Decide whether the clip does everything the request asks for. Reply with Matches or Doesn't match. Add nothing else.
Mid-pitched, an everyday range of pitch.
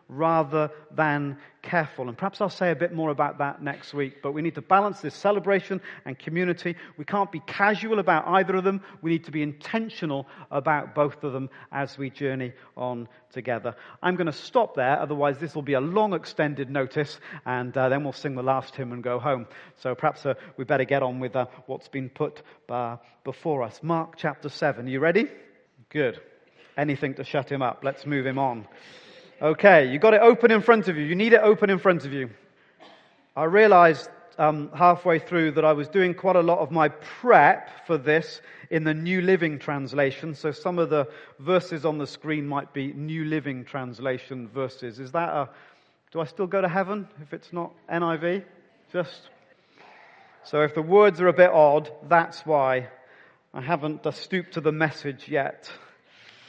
Matches